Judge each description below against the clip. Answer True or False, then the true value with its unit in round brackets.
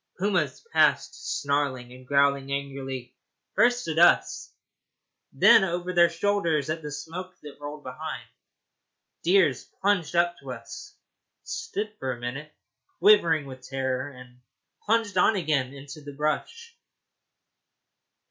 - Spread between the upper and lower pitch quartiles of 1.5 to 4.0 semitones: False (5.0 semitones)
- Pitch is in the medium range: True (150 Hz)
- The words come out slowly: True (130 wpm)